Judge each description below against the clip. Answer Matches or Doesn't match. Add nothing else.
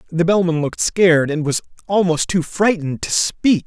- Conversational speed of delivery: Matches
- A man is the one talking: Matches